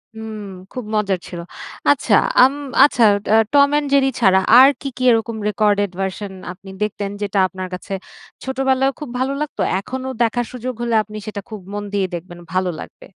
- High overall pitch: Yes, high, 215 Hz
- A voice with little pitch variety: No, average, 4.7 semitones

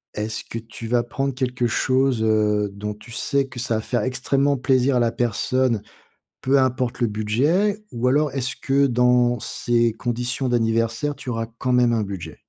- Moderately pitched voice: No, low, 120 Hz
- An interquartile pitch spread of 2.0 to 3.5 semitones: Yes, narrow, 2.5 semitones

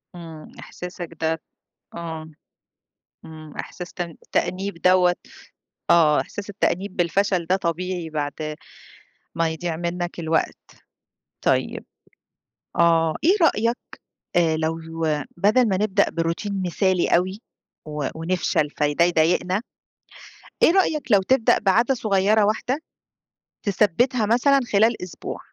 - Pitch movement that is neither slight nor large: Yes, average, 3.9 semitones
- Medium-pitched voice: Yes, medium, 180 Hz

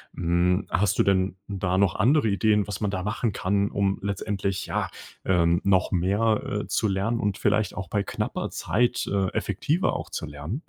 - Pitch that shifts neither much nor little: No, narrow, 2.1 semitones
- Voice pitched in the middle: No, low, 100 Hz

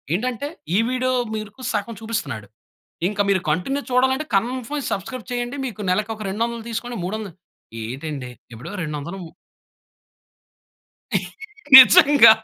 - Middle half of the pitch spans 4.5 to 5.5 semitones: Yes, average, 4.8 semitones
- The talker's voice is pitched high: Yes, high, 220 Hz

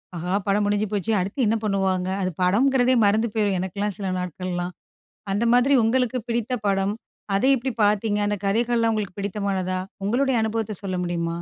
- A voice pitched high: Yes, high, 205 Hz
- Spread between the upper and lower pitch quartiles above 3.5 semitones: No, average, 3.2 semitones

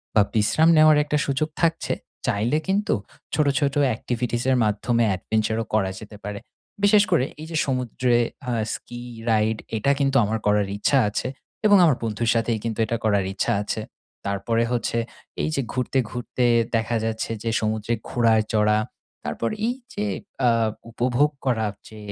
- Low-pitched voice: Yes, low, 115 Hz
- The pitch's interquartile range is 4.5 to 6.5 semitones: No, average, 4.0 semitones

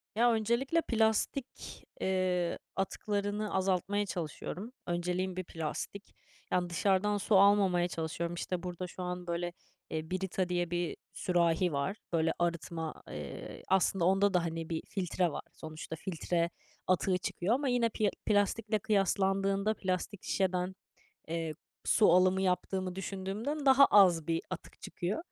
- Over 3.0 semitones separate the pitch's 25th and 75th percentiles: No, average, 2.7 semitones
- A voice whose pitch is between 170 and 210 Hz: Yes, medium, 185 Hz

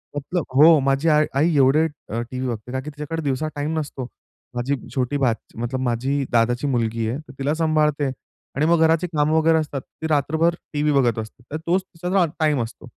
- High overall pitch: No, medium, 145 Hz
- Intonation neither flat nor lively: Yes, average, 3.6 semitones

